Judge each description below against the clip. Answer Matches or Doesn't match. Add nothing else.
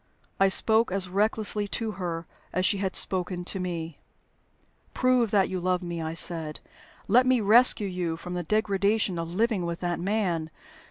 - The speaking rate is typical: Matches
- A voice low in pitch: Doesn't match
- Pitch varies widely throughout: Doesn't match